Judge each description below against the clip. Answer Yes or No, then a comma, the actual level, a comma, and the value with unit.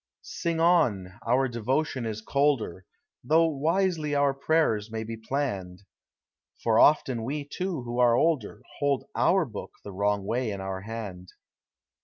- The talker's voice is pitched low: Yes, low, 125 Hz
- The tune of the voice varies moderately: No, wide, 5.8 semitones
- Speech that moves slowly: No, average, 145 wpm